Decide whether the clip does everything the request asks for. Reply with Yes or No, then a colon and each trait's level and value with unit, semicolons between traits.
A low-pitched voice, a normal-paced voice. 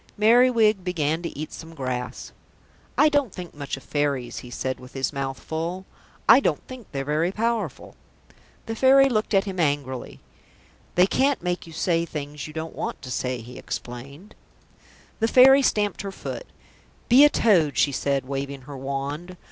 No: medium, 165 Hz; average, 170 wpm